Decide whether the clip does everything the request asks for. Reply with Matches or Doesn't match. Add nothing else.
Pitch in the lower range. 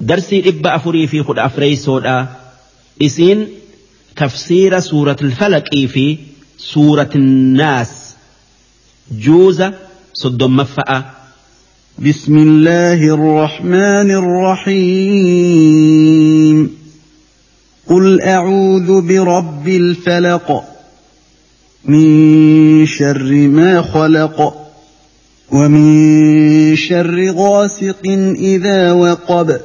Doesn't match